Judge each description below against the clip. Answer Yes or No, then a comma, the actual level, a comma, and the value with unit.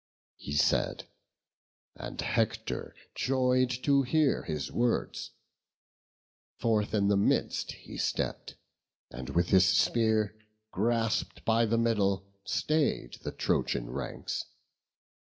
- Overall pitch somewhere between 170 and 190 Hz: No, low, 110 Hz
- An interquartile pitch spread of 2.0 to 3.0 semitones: No, average, 4.2 semitones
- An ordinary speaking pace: No, slow, 105 wpm